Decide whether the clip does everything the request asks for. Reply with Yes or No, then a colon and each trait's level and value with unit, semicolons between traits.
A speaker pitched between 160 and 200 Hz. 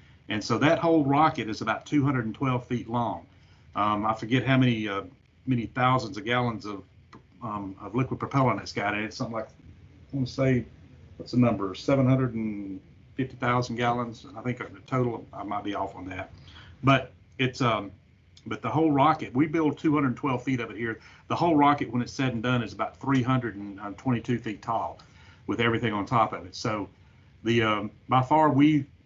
No: low, 120 Hz